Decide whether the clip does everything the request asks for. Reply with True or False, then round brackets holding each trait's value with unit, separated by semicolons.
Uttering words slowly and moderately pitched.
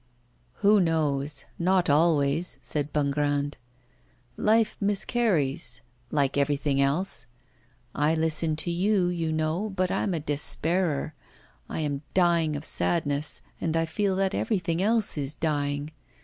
True (125 wpm; 160 Hz)